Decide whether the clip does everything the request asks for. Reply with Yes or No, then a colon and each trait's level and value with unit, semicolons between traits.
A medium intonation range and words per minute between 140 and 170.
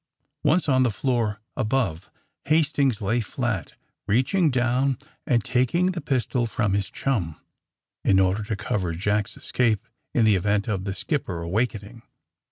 Yes: average, 4.5 semitones; average, 145 wpm